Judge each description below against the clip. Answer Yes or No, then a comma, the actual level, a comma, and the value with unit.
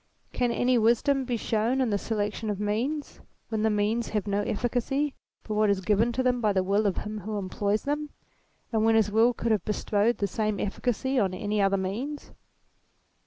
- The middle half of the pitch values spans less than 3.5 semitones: Yes, average, 2.9 semitones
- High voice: Yes, high, 220 Hz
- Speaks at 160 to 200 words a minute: Yes, average, 195 wpm